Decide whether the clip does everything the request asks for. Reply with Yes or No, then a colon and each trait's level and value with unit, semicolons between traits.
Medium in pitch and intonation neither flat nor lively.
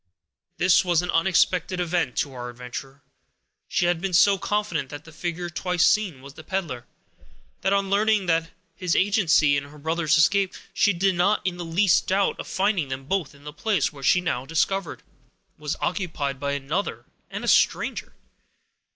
Yes: medium, 175 Hz; average, 4.8 semitones